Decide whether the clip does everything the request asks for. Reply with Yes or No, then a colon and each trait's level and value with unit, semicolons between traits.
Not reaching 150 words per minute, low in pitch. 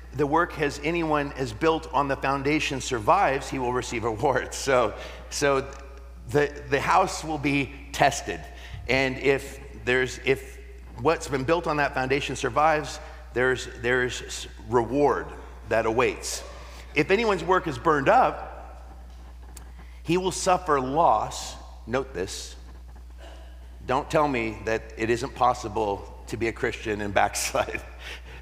Yes: slow, 135 wpm; low, 130 Hz